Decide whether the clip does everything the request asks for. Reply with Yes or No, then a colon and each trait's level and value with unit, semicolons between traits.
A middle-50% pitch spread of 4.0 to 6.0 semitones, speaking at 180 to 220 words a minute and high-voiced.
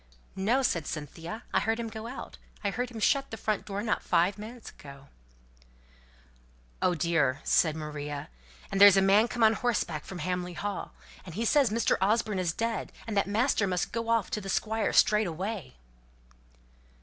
Yes: average, 4.5 semitones; average, 185 wpm; high, 205 Hz